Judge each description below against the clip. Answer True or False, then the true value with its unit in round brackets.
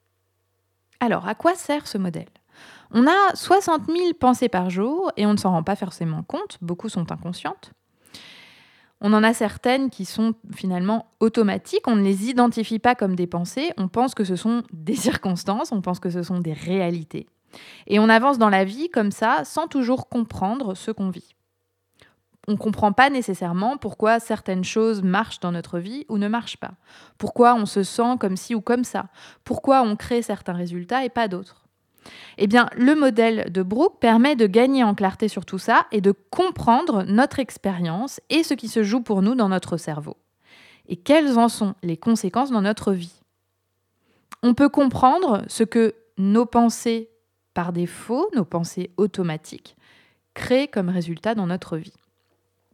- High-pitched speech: True (215 Hz)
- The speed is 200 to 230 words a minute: False (180 wpm)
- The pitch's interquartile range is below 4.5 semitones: False (4.9 semitones)